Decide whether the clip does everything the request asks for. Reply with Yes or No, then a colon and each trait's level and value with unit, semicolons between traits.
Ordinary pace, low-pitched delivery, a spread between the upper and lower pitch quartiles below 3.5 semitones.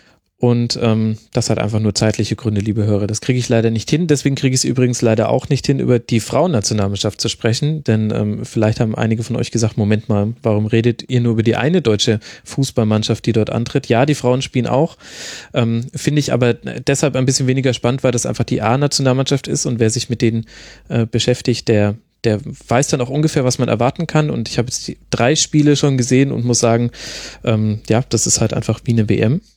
No: fast, 220 wpm; low, 120 Hz; average, 3.0 semitones